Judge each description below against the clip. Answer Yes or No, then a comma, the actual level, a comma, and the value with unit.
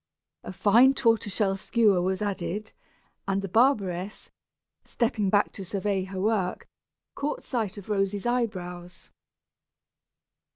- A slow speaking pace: Yes, slow, 120 wpm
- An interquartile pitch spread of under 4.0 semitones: Yes, average, 2.9 semitones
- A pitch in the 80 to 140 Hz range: No, high, 200 Hz